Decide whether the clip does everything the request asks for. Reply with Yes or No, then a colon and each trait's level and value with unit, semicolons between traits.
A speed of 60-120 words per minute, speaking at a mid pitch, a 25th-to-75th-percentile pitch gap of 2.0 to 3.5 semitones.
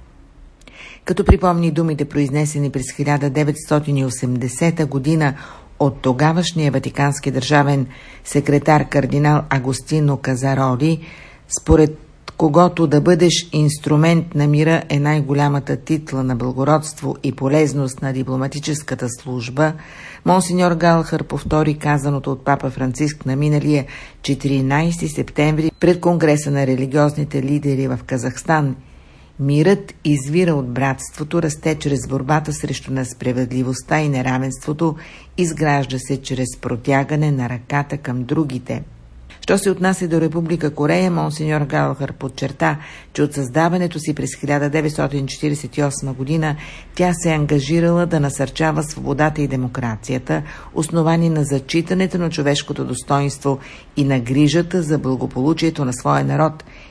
Yes: slow, 115 wpm; medium, 145 Hz; average, 2.7 semitones